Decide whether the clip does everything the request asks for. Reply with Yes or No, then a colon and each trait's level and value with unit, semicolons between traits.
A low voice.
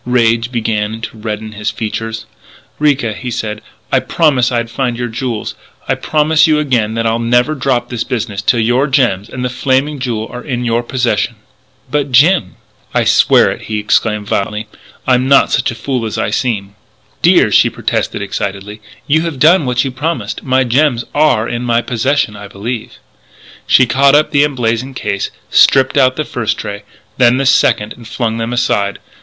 Yes: low, 120 Hz